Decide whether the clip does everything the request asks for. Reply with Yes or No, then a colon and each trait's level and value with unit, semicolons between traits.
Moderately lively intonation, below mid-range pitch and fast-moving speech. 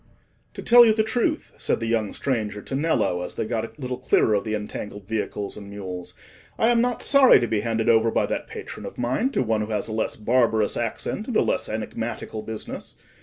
Yes: average, 4.1 semitones; low, 115 Hz; fast, 220 wpm